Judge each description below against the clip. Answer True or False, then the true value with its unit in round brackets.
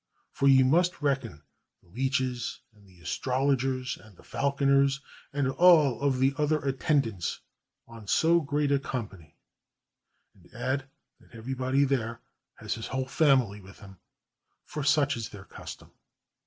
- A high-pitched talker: False (130 Hz)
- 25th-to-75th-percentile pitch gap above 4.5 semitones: False (3.5 semitones)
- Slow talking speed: False (145 wpm)